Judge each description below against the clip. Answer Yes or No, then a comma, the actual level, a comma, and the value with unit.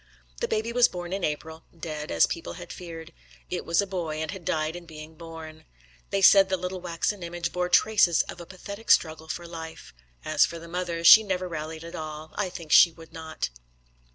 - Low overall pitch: No, medium, 170 Hz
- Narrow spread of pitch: Yes, narrow, 2.3 semitones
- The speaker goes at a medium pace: No, fast, 210 wpm